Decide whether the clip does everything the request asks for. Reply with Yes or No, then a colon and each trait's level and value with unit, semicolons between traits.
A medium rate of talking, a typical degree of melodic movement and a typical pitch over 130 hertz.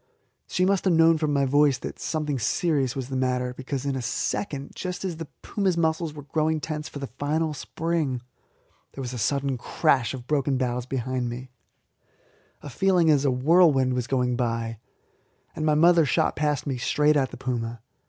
Yes: average, 190 wpm; average, 3.8 semitones; medium, 140 Hz